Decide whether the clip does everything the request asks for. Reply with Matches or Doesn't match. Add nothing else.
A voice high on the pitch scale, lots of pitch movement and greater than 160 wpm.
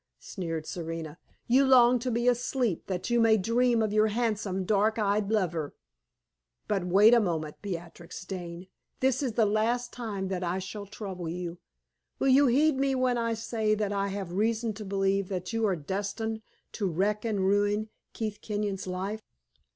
Doesn't match